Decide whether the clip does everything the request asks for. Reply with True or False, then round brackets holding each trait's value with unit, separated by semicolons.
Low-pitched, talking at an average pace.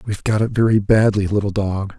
False (105 Hz; 210 wpm)